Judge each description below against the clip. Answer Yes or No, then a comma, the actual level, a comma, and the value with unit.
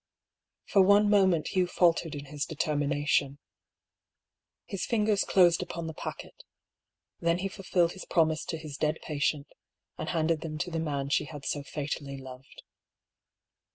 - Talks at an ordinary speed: Yes, average, 150 wpm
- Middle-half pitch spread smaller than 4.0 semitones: Yes, average, 3.5 semitones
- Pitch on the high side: No, medium, 160 Hz